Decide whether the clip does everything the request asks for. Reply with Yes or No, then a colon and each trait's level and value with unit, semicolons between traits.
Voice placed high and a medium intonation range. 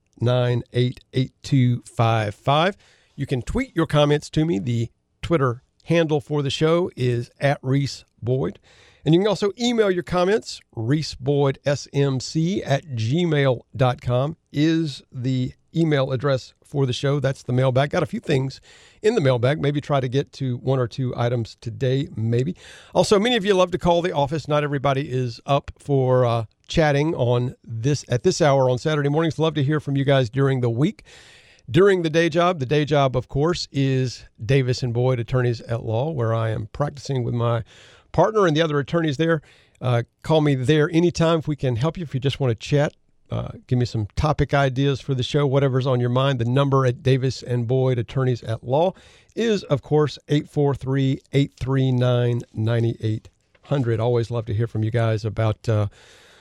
No: low, 135 Hz; average, 3.5 semitones